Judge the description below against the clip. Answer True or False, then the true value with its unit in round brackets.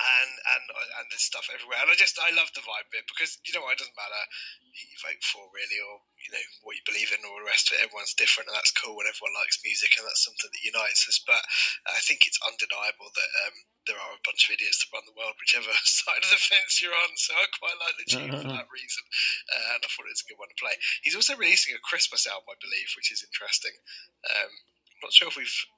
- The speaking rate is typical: False (265 wpm)